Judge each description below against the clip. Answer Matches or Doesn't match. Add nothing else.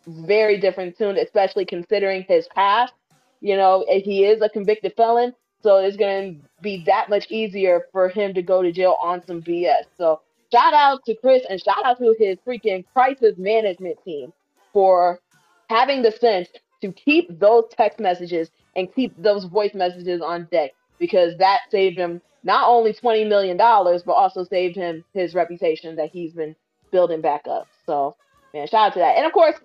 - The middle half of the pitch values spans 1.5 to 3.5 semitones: Doesn't match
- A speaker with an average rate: Matches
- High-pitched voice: Matches